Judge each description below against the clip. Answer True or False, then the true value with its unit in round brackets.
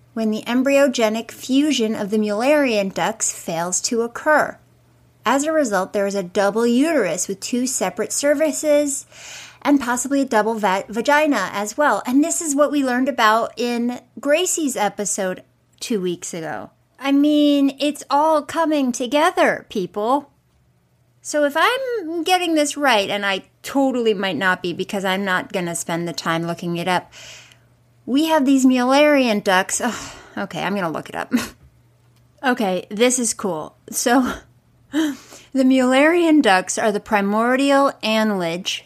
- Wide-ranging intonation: True (6.2 semitones)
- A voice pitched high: True (240 Hz)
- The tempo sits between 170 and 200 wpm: False (150 wpm)